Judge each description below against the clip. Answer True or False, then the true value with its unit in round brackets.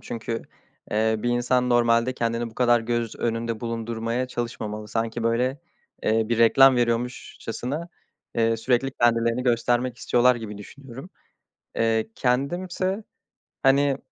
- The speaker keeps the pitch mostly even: True (1.7 semitones)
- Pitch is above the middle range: False (120 Hz)